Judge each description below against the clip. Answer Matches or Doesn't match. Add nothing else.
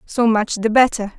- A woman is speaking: Matches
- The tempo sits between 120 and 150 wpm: Doesn't match